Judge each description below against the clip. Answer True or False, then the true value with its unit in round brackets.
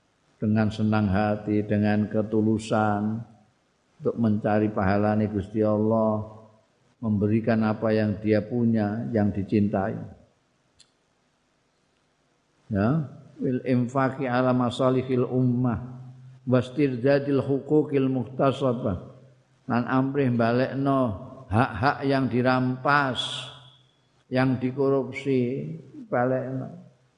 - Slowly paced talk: True (80 wpm)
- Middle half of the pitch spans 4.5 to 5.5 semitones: False (3.4 semitones)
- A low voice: True (125 Hz)